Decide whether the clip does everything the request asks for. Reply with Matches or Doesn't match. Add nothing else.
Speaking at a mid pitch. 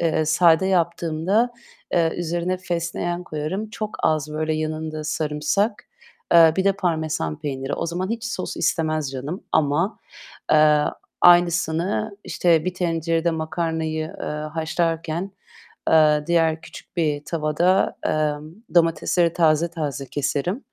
Matches